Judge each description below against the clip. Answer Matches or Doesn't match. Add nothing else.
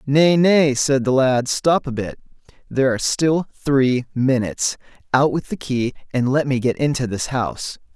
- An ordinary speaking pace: Matches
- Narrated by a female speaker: Doesn't match